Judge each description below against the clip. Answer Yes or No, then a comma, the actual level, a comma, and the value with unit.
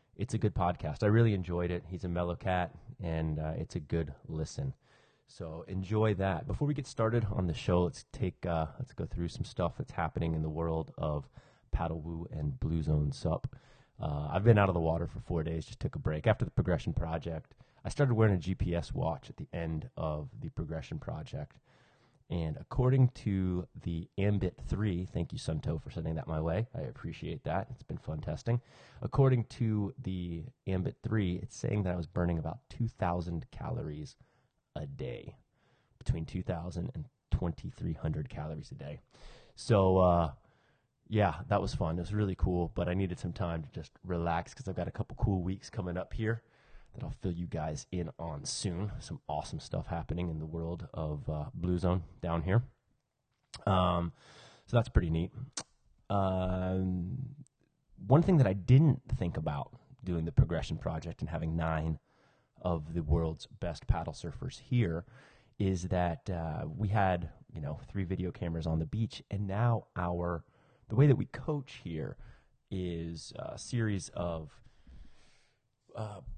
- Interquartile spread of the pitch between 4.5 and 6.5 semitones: Yes, average, 5.3 semitones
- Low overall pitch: Yes, very low, 95 Hz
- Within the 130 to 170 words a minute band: No, average, 180 wpm